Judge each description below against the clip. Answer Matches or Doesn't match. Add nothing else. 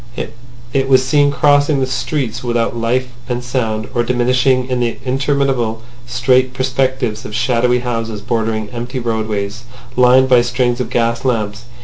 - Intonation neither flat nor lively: Doesn't match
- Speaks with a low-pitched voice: Matches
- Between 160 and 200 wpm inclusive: Doesn't match